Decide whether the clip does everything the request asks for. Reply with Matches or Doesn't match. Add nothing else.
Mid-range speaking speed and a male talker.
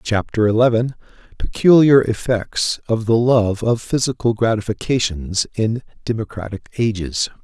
Doesn't match